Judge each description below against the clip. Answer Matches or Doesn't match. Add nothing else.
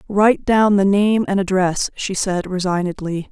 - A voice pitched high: Matches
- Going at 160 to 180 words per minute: Matches